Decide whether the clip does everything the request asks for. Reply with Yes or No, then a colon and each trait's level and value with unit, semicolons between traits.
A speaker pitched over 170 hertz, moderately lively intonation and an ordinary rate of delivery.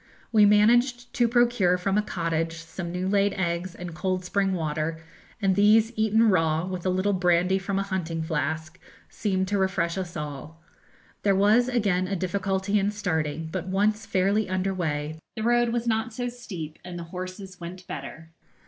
Yes: high, 190 Hz; average, 3.5 semitones; average, 175 wpm